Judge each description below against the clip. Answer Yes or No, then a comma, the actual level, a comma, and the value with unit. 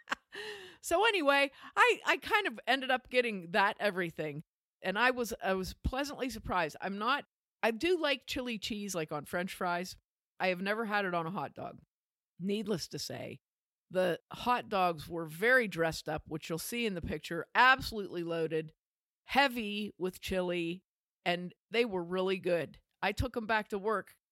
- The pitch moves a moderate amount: No, wide, 5.7 semitones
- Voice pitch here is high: Yes, high, 200 Hz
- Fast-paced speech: No, average, 175 wpm